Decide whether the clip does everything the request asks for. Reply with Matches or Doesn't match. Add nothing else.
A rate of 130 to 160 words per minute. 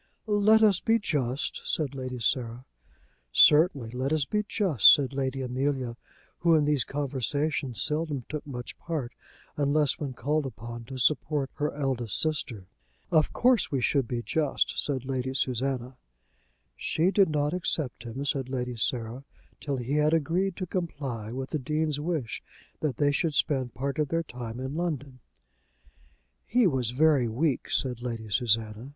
Matches